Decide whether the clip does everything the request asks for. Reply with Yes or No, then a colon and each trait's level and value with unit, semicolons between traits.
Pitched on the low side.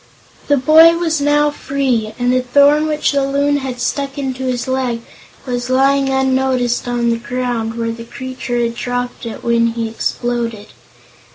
No: very high, 255 Hz